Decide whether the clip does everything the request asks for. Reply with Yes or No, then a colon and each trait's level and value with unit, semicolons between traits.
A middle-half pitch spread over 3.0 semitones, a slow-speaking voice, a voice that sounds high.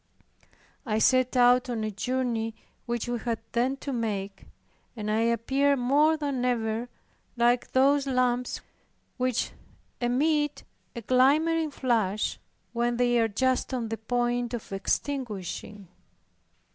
No: narrow, 2.4 semitones; slow, 125 wpm; high, 245 Hz